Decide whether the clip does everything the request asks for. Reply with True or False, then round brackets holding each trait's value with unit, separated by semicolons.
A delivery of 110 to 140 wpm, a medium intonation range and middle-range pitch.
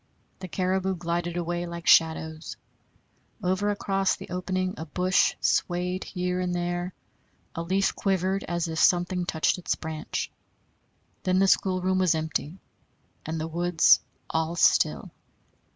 False (135 wpm; 1.7 semitones; 180 Hz)